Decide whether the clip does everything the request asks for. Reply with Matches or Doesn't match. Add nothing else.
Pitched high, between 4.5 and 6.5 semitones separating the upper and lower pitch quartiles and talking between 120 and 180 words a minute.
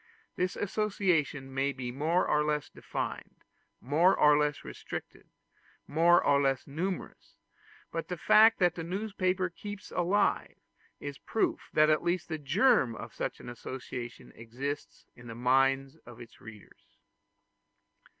Doesn't match